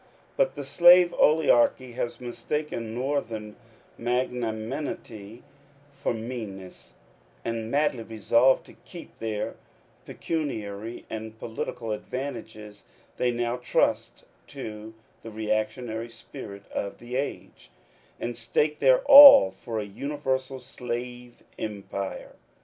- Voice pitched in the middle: No, low, 120 Hz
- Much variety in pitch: No, average, 3.4 semitones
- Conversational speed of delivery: No, slow, 105 wpm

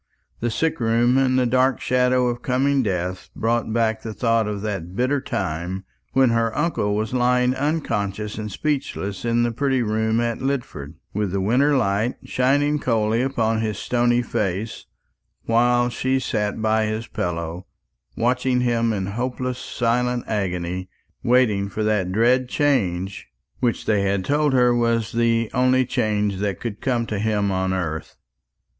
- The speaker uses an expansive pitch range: No, average, 3.5 semitones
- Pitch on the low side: Yes, low, 115 Hz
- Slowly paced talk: No, average, 155 wpm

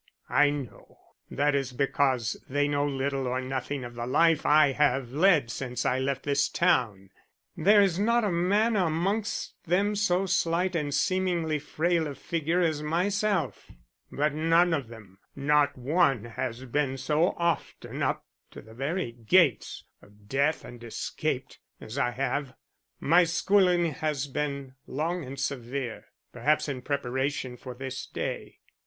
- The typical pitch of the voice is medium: Yes, medium, 145 Hz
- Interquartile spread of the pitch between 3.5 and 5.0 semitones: Yes, average, 4.6 semitones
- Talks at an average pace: Yes, average, 150 wpm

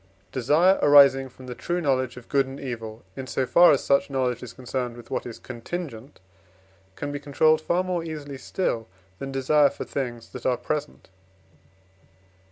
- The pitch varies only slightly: No, average, 3.0 semitones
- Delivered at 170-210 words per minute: Yes, average, 175 wpm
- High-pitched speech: No, low, 135 Hz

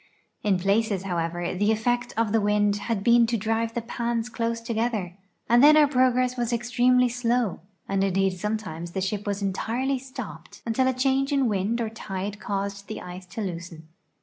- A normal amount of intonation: Yes, average, 3.7 semitones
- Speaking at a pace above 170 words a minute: Yes, average, 180 wpm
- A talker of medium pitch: No, high, 220 Hz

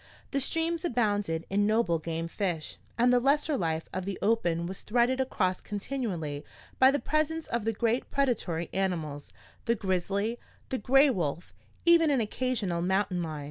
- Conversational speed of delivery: Yes, average, 160 wpm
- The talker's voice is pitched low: No, high, 210 Hz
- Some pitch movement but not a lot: No, wide, 6.8 semitones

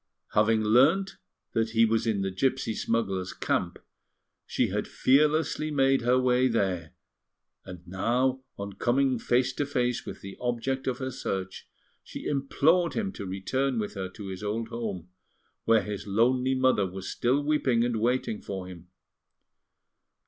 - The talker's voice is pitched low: Yes, low, 120 Hz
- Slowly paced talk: No, average, 155 wpm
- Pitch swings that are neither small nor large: Yes, average, 4.7 semitones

